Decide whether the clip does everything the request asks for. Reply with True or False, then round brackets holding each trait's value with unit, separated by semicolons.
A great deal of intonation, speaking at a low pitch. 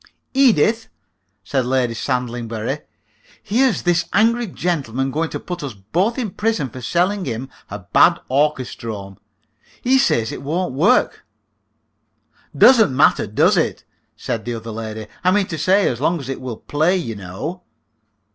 False (8.0 semitones; 145 Hz)